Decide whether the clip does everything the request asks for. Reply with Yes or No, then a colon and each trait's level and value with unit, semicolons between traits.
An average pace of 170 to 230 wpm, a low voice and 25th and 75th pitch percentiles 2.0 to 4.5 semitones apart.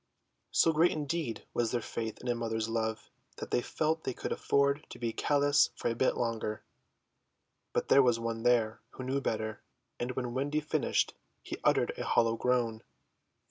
Yes: average, 180 wpm; low, 120 Hz; average, 3.7 semitones